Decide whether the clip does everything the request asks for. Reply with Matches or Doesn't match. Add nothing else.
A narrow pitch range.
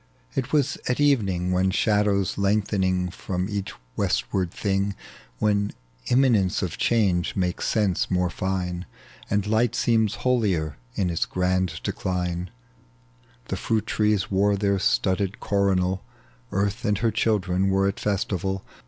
Matches